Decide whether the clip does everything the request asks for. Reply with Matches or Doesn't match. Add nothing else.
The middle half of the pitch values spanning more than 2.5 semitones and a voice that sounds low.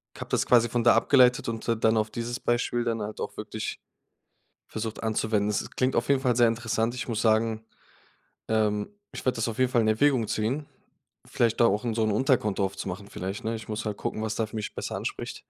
Doesn't match